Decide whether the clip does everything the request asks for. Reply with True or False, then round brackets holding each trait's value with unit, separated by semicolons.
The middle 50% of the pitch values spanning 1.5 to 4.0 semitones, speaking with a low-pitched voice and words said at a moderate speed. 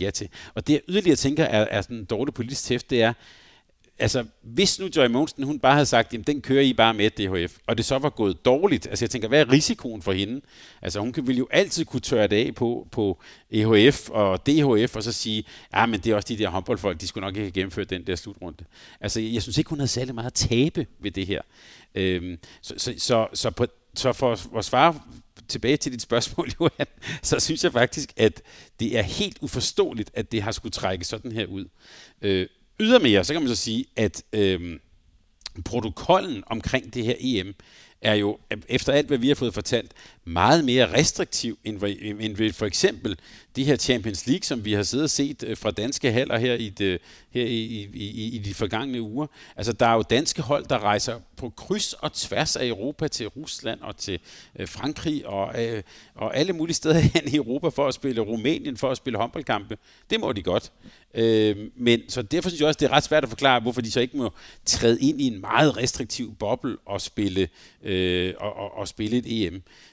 False (4.9 semitones; 115 Hz; 215 wpm)